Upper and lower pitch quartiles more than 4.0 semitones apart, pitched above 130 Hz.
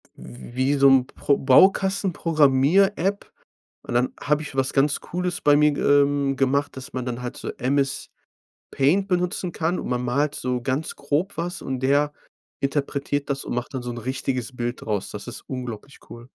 No: average, 2.8 semitones; medium, 140 Hz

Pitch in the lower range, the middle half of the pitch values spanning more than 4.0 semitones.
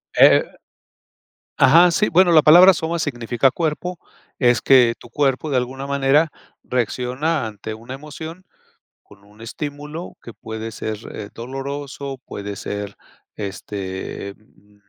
Yes: low, 130 Hz; wide, 5.6 semitones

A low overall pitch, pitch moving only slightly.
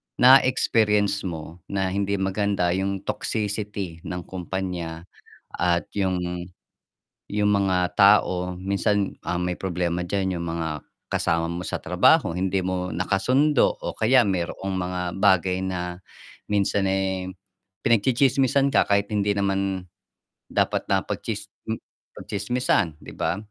Yes: very low, 95 Hz; narrow, 2.3 semitones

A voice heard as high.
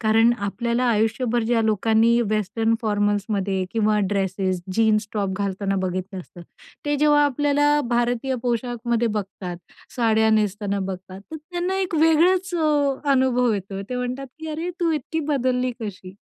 Yes: high, 230 Hz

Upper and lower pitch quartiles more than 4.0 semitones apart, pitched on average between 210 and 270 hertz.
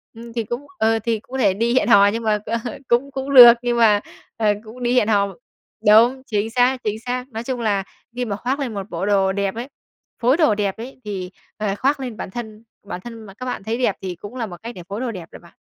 No: average, 3.2 semitones; high, 225 Hz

